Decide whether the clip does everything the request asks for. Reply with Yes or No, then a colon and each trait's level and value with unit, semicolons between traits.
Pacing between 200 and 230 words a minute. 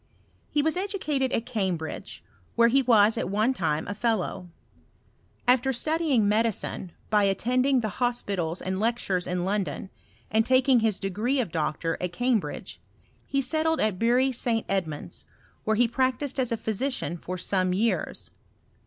No: average, 155 wpm